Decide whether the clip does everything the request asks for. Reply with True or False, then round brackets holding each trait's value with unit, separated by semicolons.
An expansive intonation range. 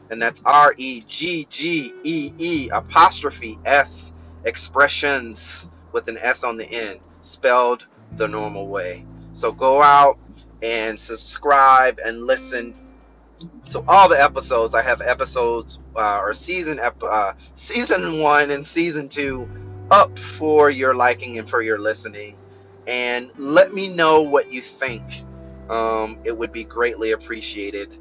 True (5.9 semitones)